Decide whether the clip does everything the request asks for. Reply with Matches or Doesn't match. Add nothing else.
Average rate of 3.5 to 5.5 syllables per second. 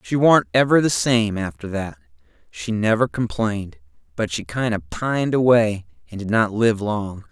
Matches